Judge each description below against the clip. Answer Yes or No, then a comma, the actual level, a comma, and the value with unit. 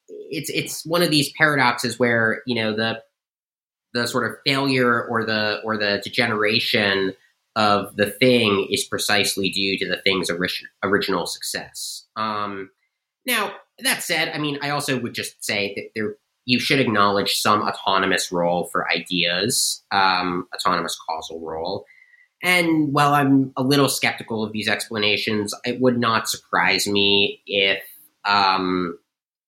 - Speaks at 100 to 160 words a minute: Yes, average, 145 wpm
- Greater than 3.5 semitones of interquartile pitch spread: Yes, average, 4.5 semitones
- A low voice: Yes, low, 110 Hz